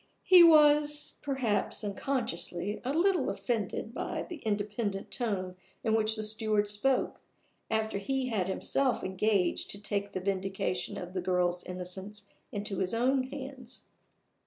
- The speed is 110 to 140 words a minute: Yes, slow, 135 wpm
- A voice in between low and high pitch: No, high, 215 Hz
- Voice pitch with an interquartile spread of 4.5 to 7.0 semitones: Yes, average, 5.2 semitones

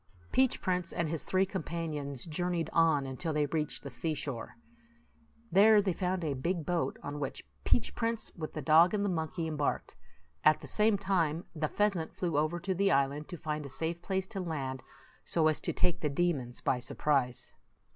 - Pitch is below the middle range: No, medium, 160 Hz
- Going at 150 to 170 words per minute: No, average, 190 wpm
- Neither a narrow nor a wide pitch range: Yes, average, 3.6 semitones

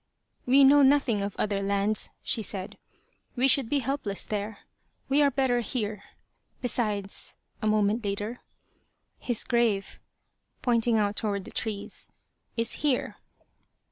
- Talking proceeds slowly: Yes, slow, 130 wpm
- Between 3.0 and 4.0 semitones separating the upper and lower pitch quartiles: Yes, average, 3.7 semitones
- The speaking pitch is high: Yes, high, 225 Hz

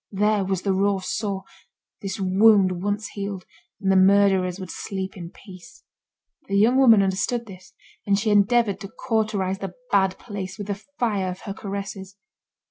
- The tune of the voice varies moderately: No, narrow, 1.5 semitones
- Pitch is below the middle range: No, high, 195 Hz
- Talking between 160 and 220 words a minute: Yes, average, 165 wpm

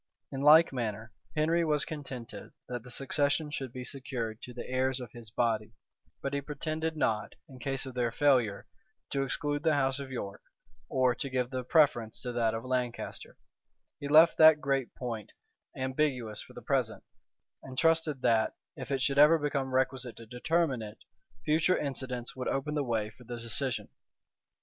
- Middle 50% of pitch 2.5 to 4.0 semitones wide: Yes, average, 3.5 semitones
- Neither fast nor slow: Yes, average, 175 wpm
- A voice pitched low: Yes, low, 130 Hz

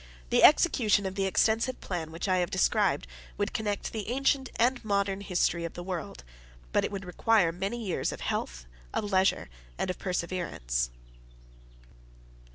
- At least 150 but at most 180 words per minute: Yes, average, 160 wpm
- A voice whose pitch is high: Yes, high, 195 Hz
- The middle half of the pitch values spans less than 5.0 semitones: Yes, average, 3.9 semitones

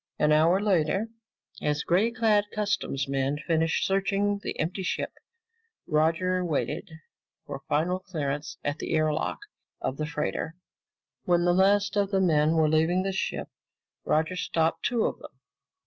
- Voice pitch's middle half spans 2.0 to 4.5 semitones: Yes, average, 4.1 semitones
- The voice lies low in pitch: No, medium, 170 Hz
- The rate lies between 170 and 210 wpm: No, average, 150 wpm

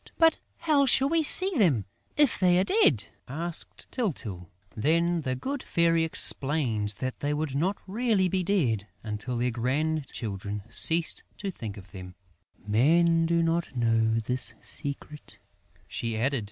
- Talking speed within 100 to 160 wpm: Yes, average, 145 wpm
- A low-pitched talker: No, medium, 150 Hz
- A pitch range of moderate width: No, wide, 7.6 semitones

